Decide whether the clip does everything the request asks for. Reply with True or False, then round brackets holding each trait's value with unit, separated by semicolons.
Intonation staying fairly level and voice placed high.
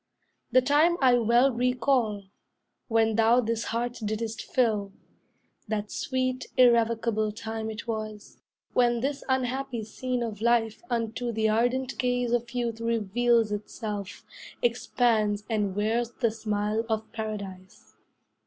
True (2.2 semitones; 230 Hz)